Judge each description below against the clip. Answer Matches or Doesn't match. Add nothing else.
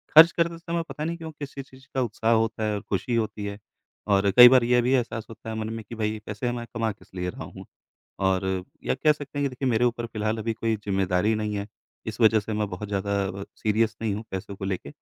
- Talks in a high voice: Doesn't match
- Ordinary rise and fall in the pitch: Matches